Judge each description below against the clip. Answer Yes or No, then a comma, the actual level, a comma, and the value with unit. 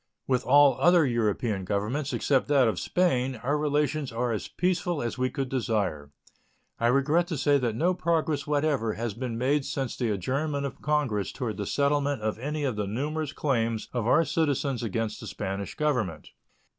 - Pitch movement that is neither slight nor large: Yes, average, 4.5 semitones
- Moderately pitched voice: No, low, 130 Hz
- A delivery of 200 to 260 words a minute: No, average, 180 wpm